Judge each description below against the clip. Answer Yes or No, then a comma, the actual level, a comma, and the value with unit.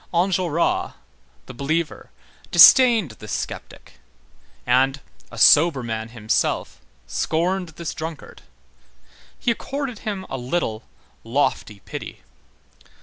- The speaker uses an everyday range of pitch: No, wide, 7.2 semitones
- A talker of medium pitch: Yes, medium, 160 Hz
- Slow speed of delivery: Yes, slow, 95 wpm